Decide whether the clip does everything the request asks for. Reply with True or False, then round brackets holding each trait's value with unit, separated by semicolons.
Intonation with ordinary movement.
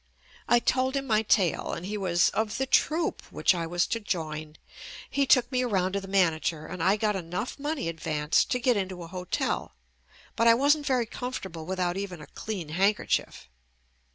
False (5.8 semitones)